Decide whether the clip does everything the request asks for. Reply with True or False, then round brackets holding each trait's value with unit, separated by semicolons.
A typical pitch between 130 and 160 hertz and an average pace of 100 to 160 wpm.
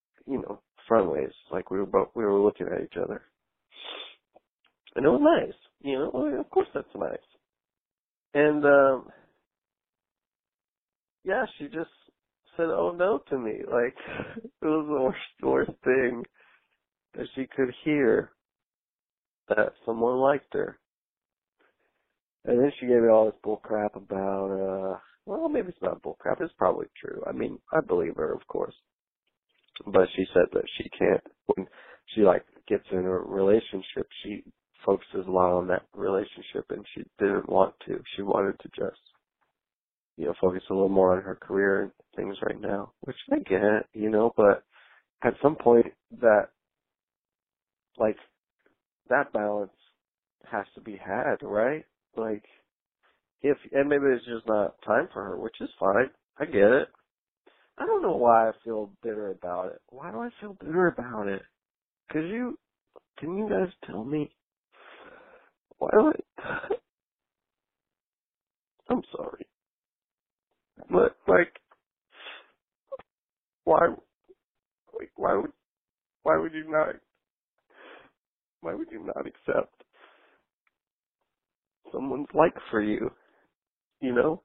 True (140 Hz; 145 wpm)